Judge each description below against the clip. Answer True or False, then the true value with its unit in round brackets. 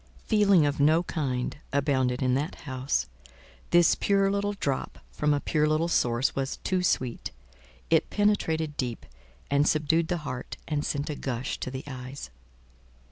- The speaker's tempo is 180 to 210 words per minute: False (155 wpm)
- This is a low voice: False (145 Hz)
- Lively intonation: False (4.2 semitones)